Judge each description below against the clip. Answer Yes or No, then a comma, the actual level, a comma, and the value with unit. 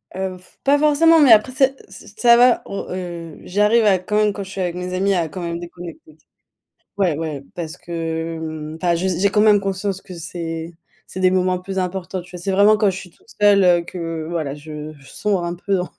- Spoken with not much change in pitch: No, average, 3.1 semitones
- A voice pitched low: No, medium, 180 Hz